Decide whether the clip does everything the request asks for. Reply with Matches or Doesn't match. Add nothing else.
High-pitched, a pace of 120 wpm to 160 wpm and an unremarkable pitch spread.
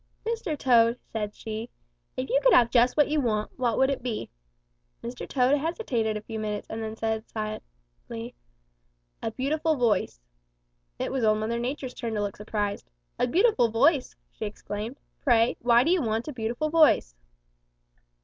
Doesn't match